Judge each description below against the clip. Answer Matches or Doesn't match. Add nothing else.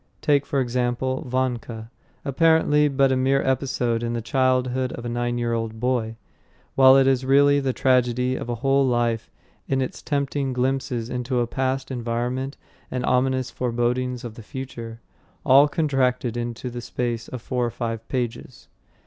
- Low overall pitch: Matches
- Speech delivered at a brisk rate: Doesn't match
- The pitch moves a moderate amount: Doesn't match